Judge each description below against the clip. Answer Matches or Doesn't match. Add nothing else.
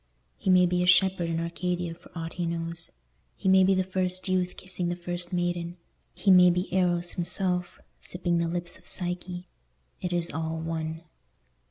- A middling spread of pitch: Doesn't match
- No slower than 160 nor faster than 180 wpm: Matches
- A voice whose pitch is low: Doesn't match